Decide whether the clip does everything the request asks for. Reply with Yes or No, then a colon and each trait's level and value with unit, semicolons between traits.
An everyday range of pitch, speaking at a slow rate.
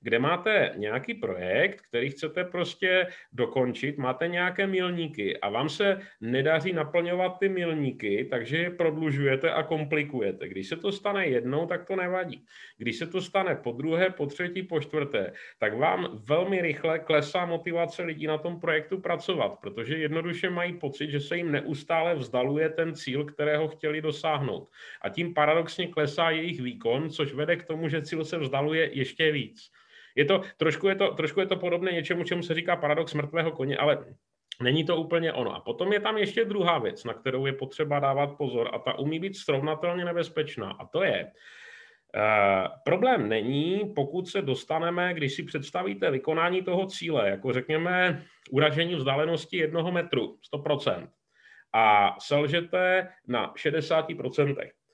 No: average, 3.4 semitones; average, 160 wpm